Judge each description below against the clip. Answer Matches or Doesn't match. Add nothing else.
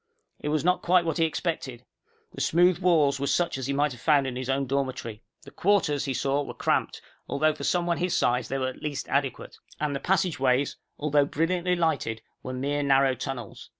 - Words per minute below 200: Doesn't match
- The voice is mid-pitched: Matches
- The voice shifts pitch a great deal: Doesn't match